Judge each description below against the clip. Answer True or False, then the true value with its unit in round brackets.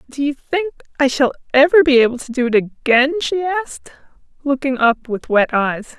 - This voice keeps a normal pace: True (190 wpm)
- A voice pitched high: True (275 Hz)